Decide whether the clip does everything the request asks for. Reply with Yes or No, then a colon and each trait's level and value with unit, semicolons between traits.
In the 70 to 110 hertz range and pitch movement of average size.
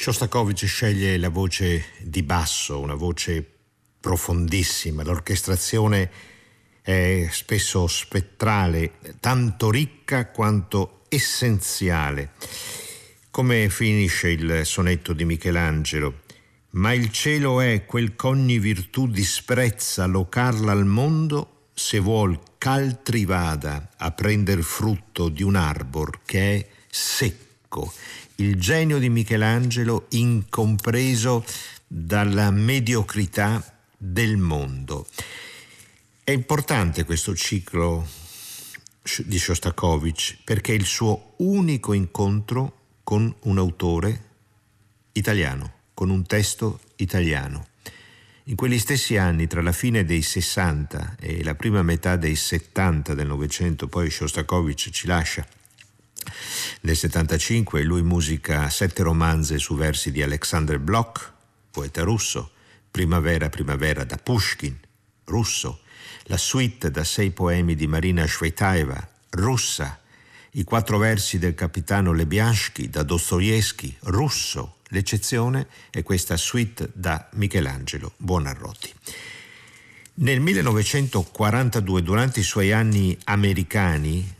Yes: low, 100 Hz; average, 4.8 semitones